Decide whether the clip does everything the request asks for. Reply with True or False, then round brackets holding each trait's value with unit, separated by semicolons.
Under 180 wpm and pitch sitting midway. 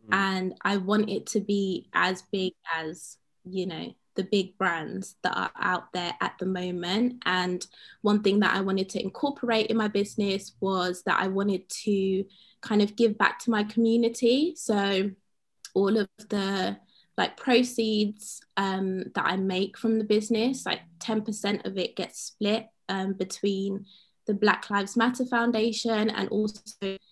False (160 wpm; 200 Hz)